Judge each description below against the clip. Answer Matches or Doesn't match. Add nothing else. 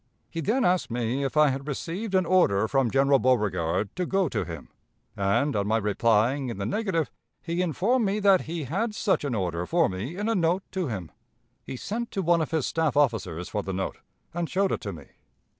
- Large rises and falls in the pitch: Matches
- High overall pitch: Doesn't match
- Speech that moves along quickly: Matches